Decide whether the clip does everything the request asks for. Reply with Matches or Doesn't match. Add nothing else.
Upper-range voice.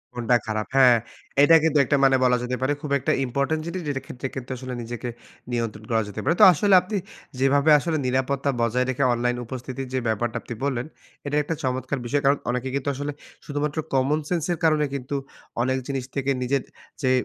Doesn't match